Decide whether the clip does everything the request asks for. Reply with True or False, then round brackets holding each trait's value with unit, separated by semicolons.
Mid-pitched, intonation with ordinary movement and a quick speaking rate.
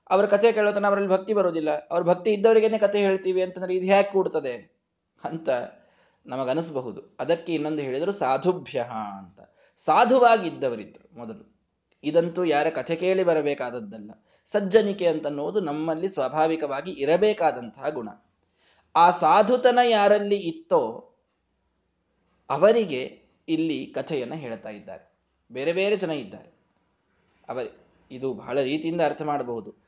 False (170 Hz; 5.8 semitones; 110 wpm)